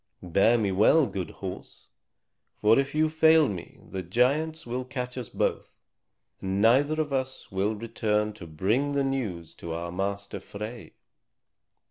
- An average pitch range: No, wide, 5.7 semitones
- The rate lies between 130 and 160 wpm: Yes, average, 150 wpm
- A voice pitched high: No, low, 115 Hz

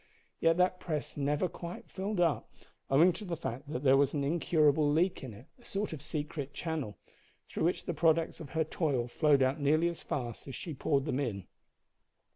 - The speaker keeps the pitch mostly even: No, average, 3.4 semitones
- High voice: No, medium, 150 Hz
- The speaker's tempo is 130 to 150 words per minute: No, average, 200 wpm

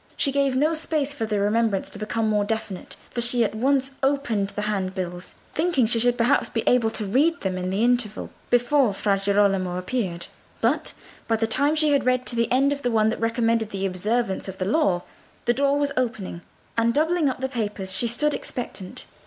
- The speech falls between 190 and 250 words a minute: Yes, fast, 205 wpm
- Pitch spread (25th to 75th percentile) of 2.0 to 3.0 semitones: No, average, 4.8 semitones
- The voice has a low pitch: No, high, 230 Hz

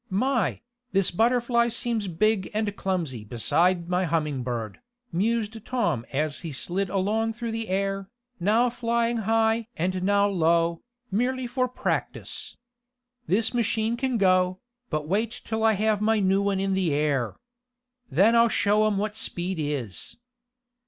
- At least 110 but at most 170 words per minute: Yes, average, 145 wpm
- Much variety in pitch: No, average, 4.6 semitones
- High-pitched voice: Yes, high, 200 Hz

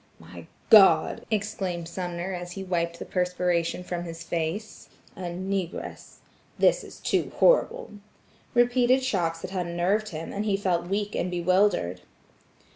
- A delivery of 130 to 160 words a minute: Yes, slow, 135 wpm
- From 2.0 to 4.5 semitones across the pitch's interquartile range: Yes, average, 2.9 semitones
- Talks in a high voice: No, medium, 180 Hz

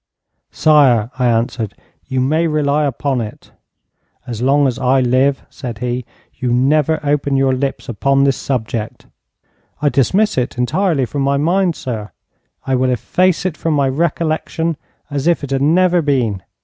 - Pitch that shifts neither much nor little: Yes, average, 3.5 semitones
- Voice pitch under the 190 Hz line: Yes, low, 135 Hz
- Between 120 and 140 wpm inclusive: No, average, 160 wpm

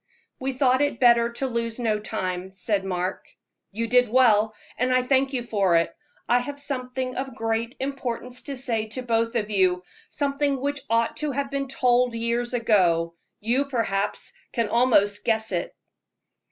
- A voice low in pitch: No, high, 235 Hz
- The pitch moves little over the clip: No, average, 3.3 semitones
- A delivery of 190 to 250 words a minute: No, average, 165 wpm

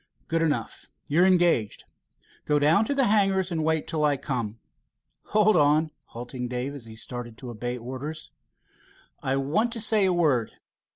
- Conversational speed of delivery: Yes, average, 165 wpm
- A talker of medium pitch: Yes, medium, 150 Hz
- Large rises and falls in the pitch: Yes, wide, 6.2 semitones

